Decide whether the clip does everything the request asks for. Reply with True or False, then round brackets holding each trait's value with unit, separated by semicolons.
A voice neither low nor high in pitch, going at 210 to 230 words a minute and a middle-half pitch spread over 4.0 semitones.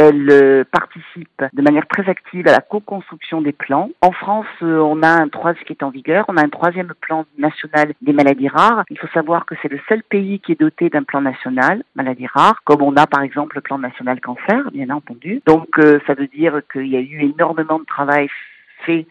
False (155 Hz; 215 wpm; 3.3 semitones)